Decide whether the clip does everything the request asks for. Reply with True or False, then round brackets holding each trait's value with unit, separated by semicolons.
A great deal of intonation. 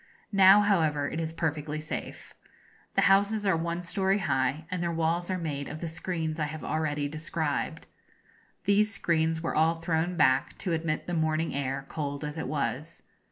False (2.4 semitones)